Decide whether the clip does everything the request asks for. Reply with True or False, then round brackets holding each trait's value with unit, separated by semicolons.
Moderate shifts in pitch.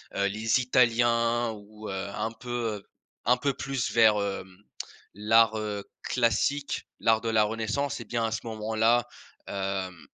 False (2.1 semitones)